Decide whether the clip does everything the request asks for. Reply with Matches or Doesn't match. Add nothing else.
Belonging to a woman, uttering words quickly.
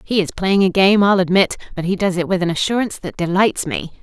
Matches